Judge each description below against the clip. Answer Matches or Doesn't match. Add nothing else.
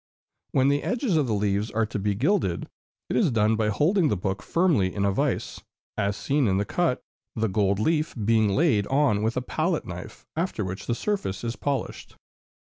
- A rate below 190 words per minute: Doesn't match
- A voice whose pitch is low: Matches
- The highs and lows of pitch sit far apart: Matches